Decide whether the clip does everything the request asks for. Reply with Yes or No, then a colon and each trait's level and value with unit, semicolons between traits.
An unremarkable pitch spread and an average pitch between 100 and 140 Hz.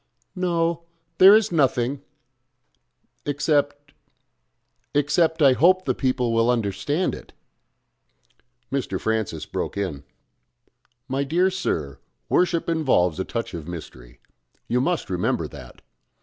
No: wide, 8.6 semitones; low, 135 Hz